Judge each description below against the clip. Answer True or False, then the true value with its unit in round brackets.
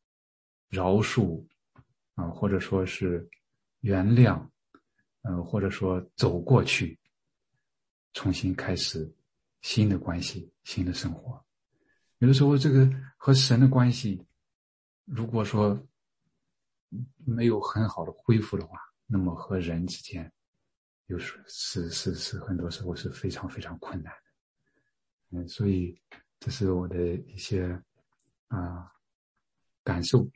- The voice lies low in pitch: True (95 Hz)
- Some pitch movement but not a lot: True (4.8 semitones)